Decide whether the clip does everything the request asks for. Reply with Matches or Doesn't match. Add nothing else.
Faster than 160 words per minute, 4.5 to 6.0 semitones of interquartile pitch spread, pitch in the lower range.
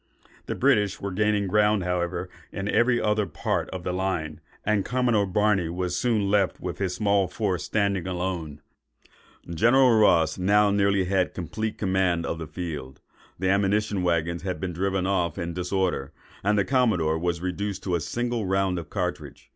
Doesn't match